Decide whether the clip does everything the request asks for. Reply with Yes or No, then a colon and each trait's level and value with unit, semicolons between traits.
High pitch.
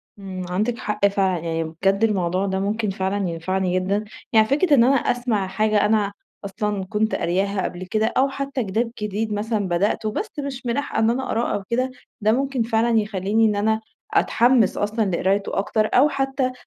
Yes: high, 210 Hz